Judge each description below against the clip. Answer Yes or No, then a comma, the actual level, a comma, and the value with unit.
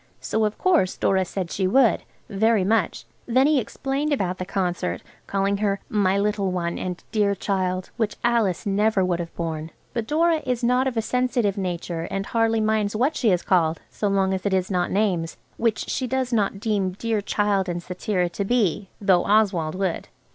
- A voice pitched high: Yes, high, 200 Hz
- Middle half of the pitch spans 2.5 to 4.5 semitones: Yes, average, 3.5 semitones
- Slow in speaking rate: No, average, 190 wpm